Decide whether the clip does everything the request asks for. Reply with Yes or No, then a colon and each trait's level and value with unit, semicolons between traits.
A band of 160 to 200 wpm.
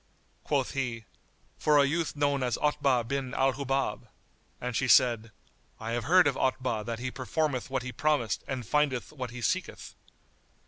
Yes: average, 170 wpm